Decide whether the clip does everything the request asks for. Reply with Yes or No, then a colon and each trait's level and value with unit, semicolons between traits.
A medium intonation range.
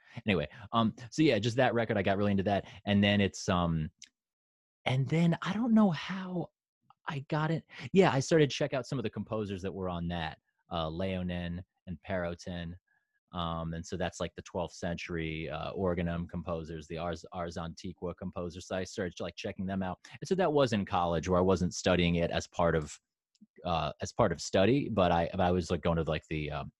Yes: average, 4.8 semitones